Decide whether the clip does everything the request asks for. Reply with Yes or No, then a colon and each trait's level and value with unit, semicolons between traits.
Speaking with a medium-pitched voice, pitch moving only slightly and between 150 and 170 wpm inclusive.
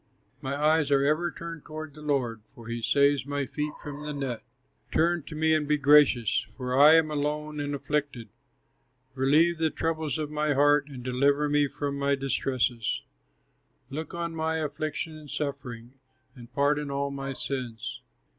Yes: medium, 145 Hz; narrow, 2.0 semitones; average, 165 wpm